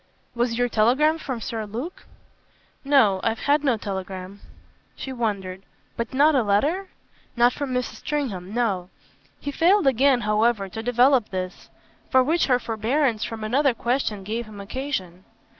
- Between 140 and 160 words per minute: Yes, average, 155 wpm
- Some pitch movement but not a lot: Yes, average, 4.6 semitones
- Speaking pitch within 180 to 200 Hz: No, high, 235 Hz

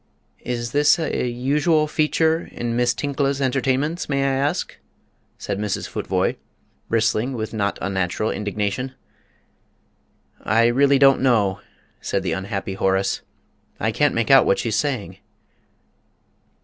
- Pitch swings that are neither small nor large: Yes, average, 4.7 semitones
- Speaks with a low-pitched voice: Yes, low, 120 Hz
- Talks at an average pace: No, slow, 125 wpm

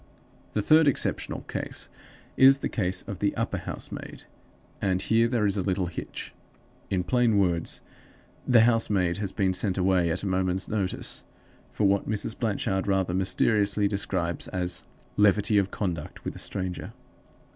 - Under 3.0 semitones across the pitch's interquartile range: Yes, narrow, 2.5 semitones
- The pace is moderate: Yes, average, 155 wpm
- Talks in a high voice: No, low, 100 Hz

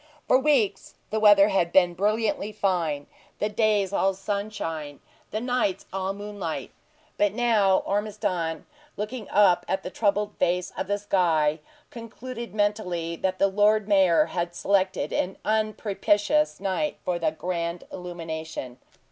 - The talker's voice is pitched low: No, high, 195 Hz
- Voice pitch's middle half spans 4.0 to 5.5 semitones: No, average, 3.2 semitones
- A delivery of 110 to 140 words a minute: Yes, slow, 135 wpm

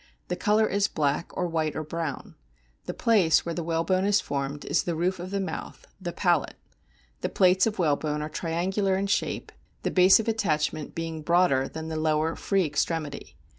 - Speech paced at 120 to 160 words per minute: No, average, 185 wpm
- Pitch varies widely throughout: No, average, 3.5 semitones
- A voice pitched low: No, medium, 170 Hz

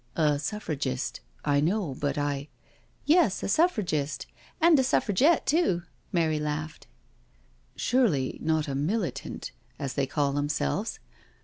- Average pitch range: No, wide, 6.7 semitones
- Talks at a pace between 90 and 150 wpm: Yes, average, 140 wpm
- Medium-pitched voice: Yes, medium, 155 Hz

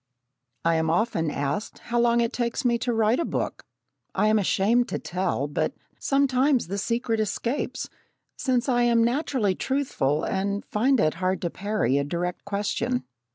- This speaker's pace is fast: No, average, 165 wpm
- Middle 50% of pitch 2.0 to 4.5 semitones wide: No, average, 5.2 semitones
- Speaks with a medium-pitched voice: No, high, 215 Hz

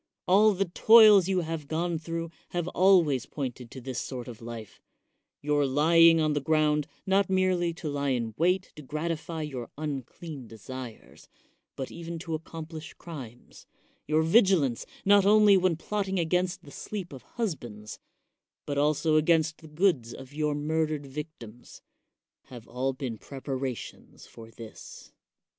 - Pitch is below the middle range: No, medium, 155 Hz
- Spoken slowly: No, average, 150 wpm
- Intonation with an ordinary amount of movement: Yes, average, 4.6 semitones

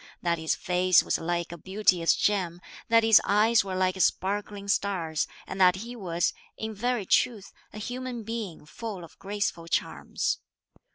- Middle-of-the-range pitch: No, high, 195 Hz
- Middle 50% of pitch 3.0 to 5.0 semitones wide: Yes, average, 3.7 semitones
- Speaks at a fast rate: No, average, 160 wpm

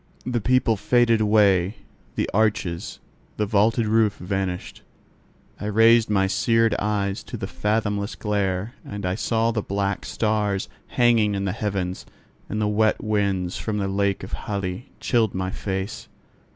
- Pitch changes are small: Yes, narrow, 2.2 semitones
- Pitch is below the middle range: Yes, low, 105 Hz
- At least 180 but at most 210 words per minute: No, average, 150 wpm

